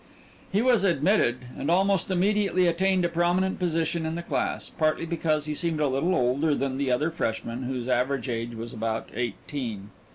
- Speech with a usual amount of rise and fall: No, wide, 5.8 semitones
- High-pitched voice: No, medium, 155 Hz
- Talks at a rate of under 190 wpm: Yes, average, 175 wpm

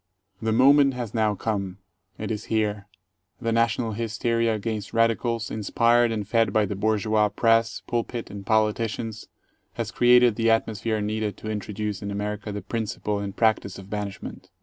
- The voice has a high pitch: No, low, 110 Hz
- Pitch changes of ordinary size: No, narrow, 1.8 semitones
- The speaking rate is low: No, average, 155 wpm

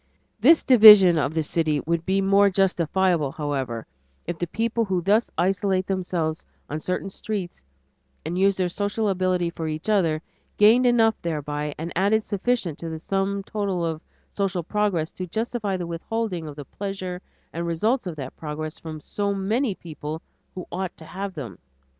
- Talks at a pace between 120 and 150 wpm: No, average, 170 wpm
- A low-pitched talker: No, medium, 185 Hz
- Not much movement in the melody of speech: No, average, 3.8 semitones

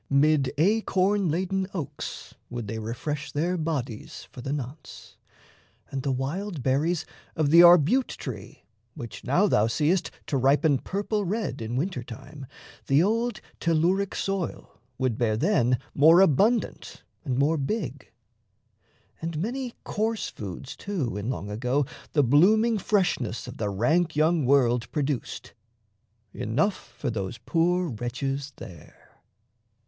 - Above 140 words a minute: No, slow, 135 wpm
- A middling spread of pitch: No, wide, 6.5 semitones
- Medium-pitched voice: Yes, medium, 150 Hz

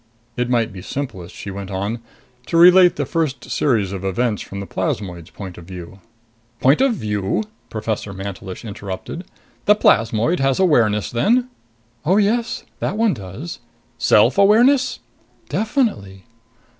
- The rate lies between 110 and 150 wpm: Yes, average, 140 wpm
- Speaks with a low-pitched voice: Yes, low, 115 Hz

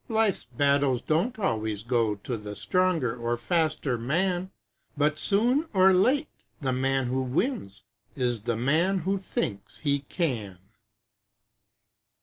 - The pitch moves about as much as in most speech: No, wide, 7.6 semitones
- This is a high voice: No, medium, 140 Hz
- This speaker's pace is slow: Yes, slow, 130 wpm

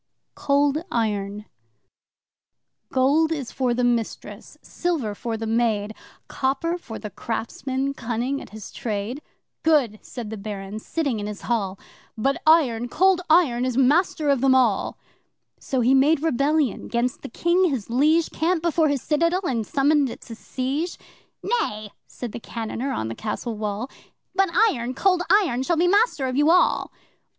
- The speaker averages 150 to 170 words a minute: Yes, average, 160 wpm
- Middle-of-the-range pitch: No, very high, 260 Hz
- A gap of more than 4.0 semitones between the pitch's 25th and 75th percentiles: Yes, wide, 5.6 semitones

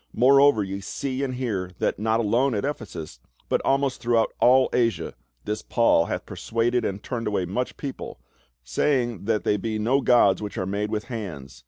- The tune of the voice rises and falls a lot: No, average, 3.9 semitones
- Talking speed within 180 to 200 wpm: Yes, average, 185 wpm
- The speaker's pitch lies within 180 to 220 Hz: No, low, 115 Hz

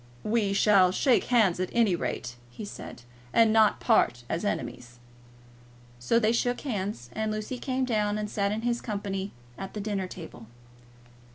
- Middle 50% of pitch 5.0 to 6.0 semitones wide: No, average, 3.4 semitones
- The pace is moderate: Yes, average, 165 wpm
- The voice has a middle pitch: No, high, 210 Hz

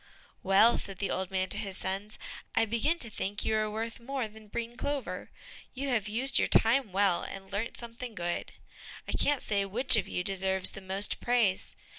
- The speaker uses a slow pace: No, average, 195 wpm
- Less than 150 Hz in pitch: No, high, 215 Hz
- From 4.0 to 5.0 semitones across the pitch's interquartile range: No, average, 3.4 semitones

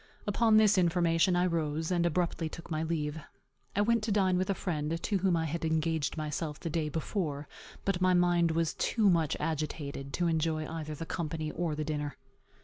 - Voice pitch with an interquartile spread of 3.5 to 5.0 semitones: No, narrow, 2.5 semitones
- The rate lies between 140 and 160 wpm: No, average, 195 wpm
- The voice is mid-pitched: Yes, medium, 165 Hz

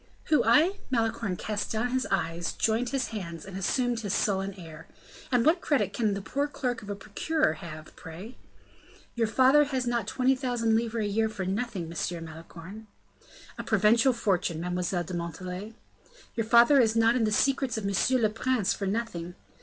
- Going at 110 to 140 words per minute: No, average, 180 wpm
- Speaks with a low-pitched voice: No, high, 220 Hz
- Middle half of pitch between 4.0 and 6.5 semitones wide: Yes, average, 4.9 semitones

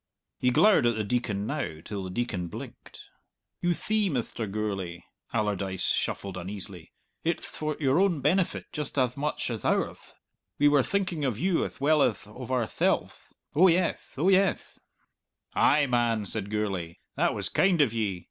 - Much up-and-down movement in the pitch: Yes, wide, 6.9 semitones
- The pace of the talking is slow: No, average, 165 wpm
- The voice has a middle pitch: No, low, 125 Hz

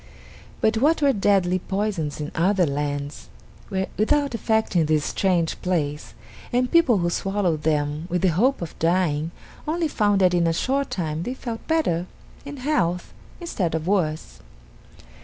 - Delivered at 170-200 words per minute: No, average, 160 wpm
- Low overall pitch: No, medium, 185 Hz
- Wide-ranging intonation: Yes, wide, 5.8 semitones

